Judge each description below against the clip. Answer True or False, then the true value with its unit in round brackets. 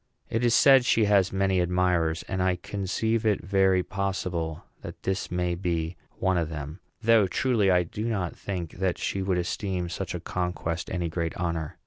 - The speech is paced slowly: False (180 wpm)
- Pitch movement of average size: False (2.1 semitones)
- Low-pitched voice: True (90 Hz)